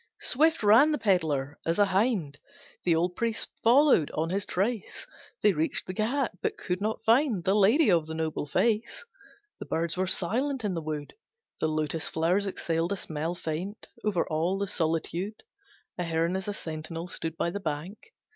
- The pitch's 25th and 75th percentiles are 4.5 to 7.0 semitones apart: Yes, average, 4.8 semitones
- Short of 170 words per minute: No, average, 180 wpm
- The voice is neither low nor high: Yes, medium, 180 Hz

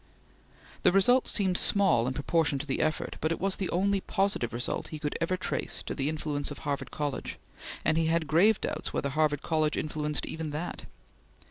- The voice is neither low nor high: Yes, medium, 155 Hz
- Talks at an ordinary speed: Yes, average, 195 wpm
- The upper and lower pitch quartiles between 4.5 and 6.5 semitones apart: No, average, 3.8 semitones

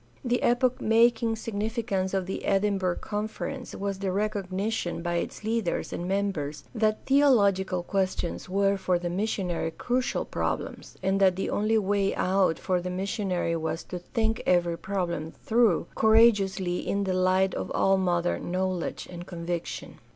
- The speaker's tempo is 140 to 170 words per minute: Yes, average, 155 wpm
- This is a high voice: Yes, high, 195 Hz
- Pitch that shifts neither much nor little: Yes, average, 3.1 semitones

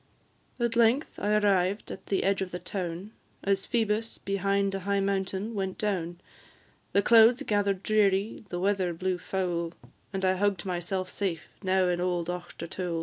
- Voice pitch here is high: Yes, high, 195 Hz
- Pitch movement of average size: No, narrow, 2.1 semitones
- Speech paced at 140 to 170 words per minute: Yes, average, 160 wpm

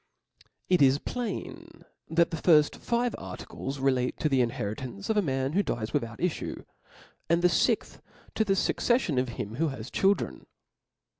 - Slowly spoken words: No, average, 160 wpm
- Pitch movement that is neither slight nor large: No, wide, 6.5 semitones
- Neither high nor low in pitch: Yes, medium, 150 Hz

